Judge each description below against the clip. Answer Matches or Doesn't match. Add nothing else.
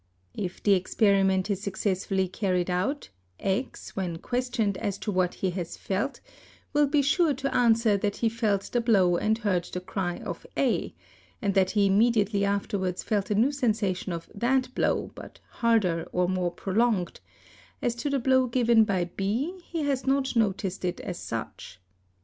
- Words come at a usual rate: Matches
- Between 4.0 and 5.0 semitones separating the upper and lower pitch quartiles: Matches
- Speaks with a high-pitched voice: Matches